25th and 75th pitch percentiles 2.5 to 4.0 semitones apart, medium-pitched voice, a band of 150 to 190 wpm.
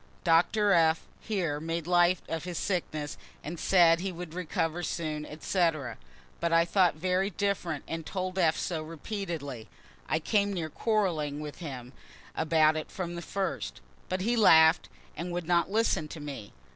Yes: average, 2.8 semitones; medium, 170 Hz; average, 160 wpm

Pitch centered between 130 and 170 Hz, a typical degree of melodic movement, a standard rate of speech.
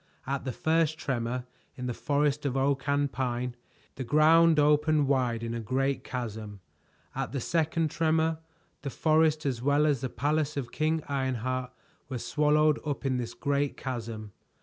Yes: medium, 140 Hz; average, 3.3 semitones; average, 165 wpm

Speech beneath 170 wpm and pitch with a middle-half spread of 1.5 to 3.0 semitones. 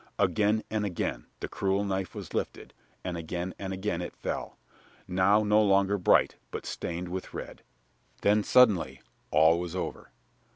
Yes: average, 155 wpm; average, 2.7 semitones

